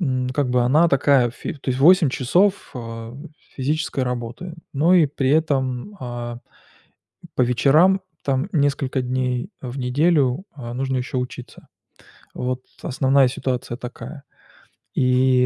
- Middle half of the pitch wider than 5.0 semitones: No, narrow, 2.6 semitones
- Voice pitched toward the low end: Yes, low, 130 Hz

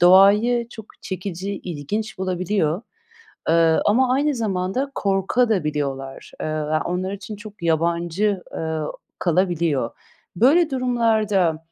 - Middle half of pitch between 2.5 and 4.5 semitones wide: No, average, 4.9 semitones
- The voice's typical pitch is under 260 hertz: Yes, high, 190 Hz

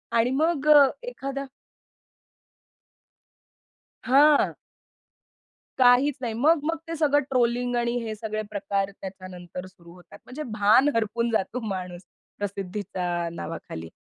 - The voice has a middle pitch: No, high, 225 Hz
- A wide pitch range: Yes, wide, 6.2 semitones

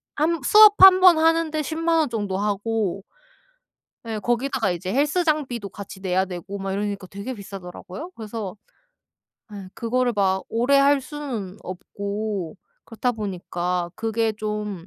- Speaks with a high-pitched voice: Yes, high, 215 Hz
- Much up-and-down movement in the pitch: Yes, wide, 6.2 semitones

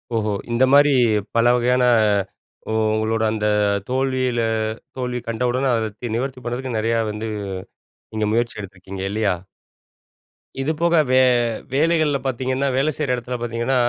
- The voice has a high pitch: No, low, 125 Hz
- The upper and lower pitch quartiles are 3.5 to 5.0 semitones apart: No, average, 2.8 semitones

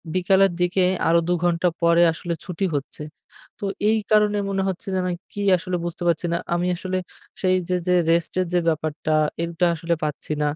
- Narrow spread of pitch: Yes, narrow, 1.8 semitones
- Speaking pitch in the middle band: Yes, medium, 175 Hz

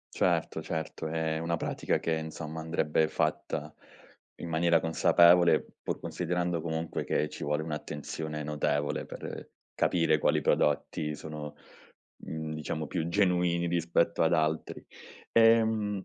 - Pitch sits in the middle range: No, very low, 80 Hz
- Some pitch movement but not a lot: No, narrow, 1.8 semitones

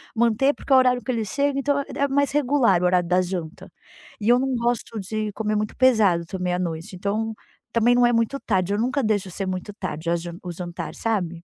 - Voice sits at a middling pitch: No, high, 215 Hz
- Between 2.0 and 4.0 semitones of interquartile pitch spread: No, average, 5.3 semitones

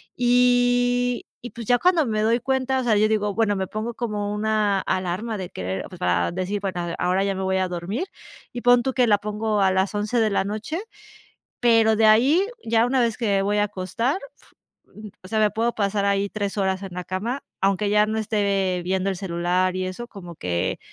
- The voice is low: No, high, 210 Hz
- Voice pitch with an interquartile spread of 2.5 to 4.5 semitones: Yes, average, 3.7 semitones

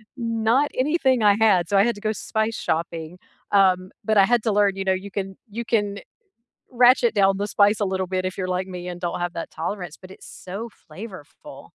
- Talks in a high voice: Yes, high, 200 Hz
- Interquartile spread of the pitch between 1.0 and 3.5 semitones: Yes, average, 3.2 semitones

